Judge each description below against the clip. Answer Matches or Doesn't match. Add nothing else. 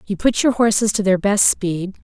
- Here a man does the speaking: Doesn't match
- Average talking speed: Doesn't match